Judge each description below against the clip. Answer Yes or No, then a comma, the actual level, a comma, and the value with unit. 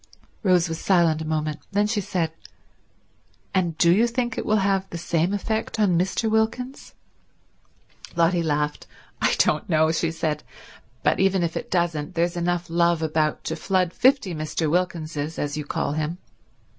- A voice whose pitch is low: No, medium, 170 Hz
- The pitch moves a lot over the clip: No, average, 3.4 semitones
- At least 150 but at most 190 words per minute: Yes, average, 165 wpm